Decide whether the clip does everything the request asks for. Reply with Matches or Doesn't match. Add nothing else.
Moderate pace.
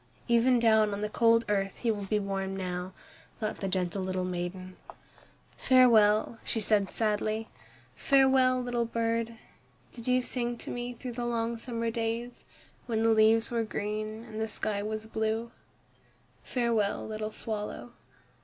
Matches